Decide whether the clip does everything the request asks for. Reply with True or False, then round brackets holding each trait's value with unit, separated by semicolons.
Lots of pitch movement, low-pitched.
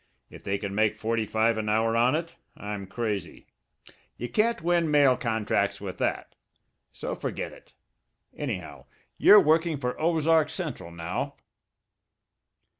True (7.3 semitones; 115 Hz)